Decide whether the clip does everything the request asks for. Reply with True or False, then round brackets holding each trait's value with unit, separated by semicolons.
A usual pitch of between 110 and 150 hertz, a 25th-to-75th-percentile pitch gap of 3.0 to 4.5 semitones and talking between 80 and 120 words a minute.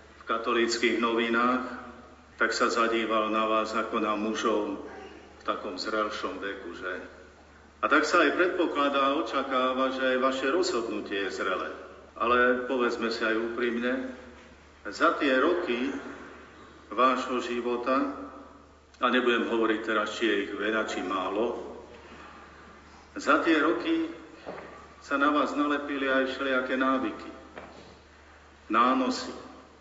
True (120 Hz; 3.4 semitones; 115 wpm)